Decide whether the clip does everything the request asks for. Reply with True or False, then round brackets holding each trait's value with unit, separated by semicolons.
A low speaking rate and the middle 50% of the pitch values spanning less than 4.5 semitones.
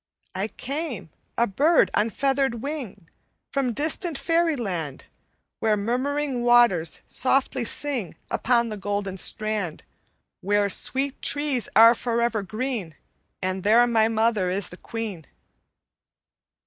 False (115 wpm; 4.9 semitones)